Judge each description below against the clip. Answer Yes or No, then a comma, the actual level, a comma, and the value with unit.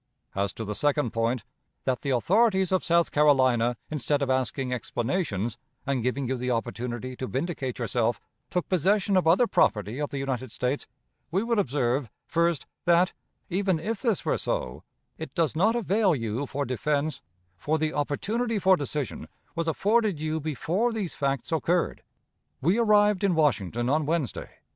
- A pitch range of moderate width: No, wide, 6.5 semitones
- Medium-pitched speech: Yes, medium, 150 Hz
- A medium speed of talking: Yes, average, 160 wpm